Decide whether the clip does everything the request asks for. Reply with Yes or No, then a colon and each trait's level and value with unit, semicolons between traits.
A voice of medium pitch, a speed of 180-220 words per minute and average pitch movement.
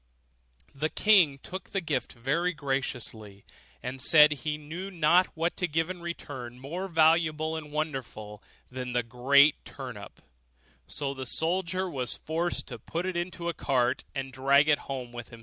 No: medium, 150 Hz; average, 165 wpm; average, 4.5 semitones